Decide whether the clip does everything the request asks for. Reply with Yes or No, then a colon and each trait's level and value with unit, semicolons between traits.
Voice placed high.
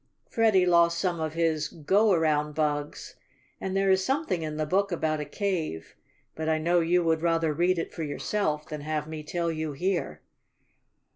No: medium, 165 Hz